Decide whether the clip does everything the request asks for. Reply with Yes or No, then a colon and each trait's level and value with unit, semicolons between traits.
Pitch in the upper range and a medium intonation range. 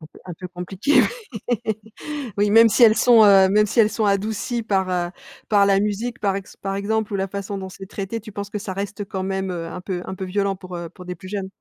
No: high, 200 Hz; narrow, 2.0 semitones